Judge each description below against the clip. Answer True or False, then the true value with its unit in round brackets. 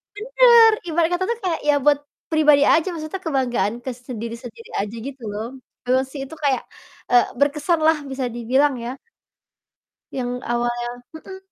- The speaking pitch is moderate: False (275 Hz)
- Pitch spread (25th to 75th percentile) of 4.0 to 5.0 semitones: True (4.7 semitones)